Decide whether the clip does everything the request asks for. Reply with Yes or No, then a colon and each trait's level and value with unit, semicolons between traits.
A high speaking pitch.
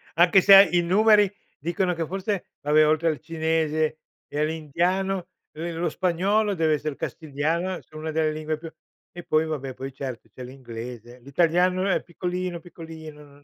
No: medium, 160 Hz